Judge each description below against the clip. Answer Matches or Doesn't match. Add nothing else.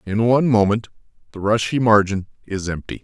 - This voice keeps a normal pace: Matches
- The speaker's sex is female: Doesn't match